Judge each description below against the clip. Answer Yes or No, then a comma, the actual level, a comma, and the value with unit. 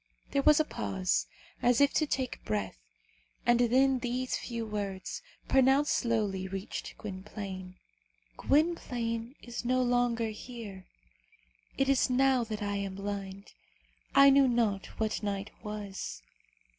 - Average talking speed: No, slow, 130 wpm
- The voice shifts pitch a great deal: No, average, 4.5 semitones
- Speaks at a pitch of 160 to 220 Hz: No, high, 230 Hz